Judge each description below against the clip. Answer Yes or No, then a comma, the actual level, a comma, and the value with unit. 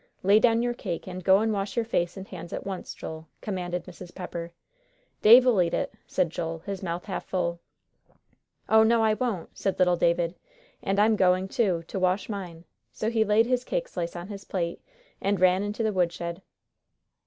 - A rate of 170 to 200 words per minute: Yes, average, 190 wpm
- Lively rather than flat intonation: No, average, 3.6 semitones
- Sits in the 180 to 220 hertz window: Yes, high, 190 Hz